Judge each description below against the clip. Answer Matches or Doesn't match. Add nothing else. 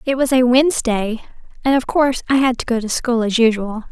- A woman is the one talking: Matches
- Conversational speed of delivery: Doesn't match